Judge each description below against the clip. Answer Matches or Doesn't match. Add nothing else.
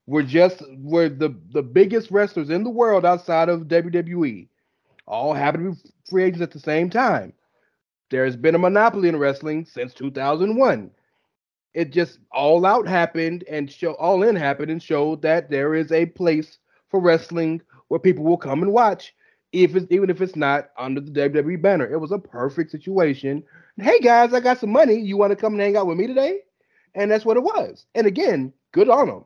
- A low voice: Doesn't match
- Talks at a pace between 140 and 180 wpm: Doesn't match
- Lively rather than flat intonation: Doesn't match